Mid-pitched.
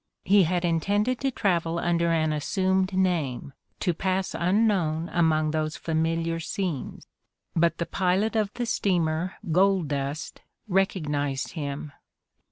Yes: medium, 170 Hz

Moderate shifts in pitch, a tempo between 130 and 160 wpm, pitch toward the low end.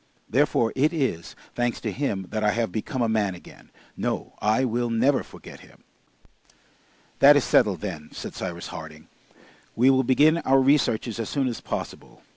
No: average, 4.2 semitones; average, 170 wpm; low, 115 Hz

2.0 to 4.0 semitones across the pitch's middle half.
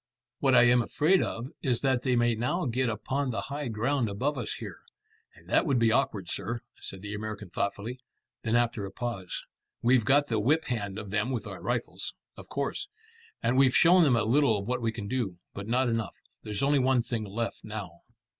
Yes: average, 3.4 semitones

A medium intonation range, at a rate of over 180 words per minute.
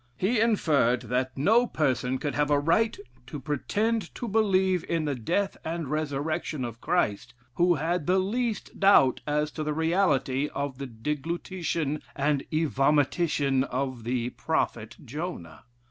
No: average, 5.0 semitones; average, 145 wpm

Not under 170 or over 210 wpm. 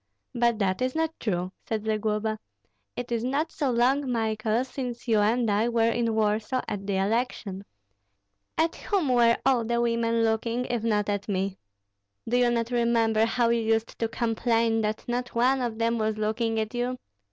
Yes: average, 180 wpm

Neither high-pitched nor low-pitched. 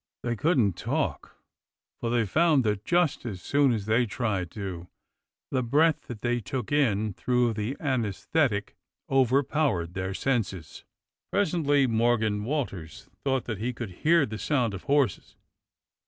No: low, 120 Hz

